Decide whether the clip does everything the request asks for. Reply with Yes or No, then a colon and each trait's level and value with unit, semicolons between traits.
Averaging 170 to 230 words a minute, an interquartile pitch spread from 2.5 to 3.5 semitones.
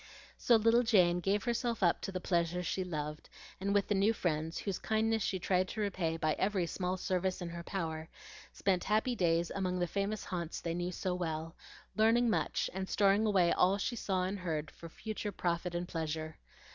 Yes: average, 195 wpm; average, 3.1 semitones